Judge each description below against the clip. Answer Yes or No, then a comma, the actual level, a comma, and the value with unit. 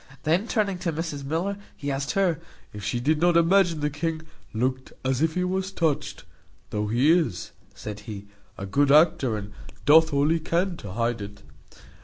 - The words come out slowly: No, average, 185 wpm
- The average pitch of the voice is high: No, medium, 150 Hz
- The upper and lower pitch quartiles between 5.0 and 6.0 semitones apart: Yes, wide, 5.6 semitones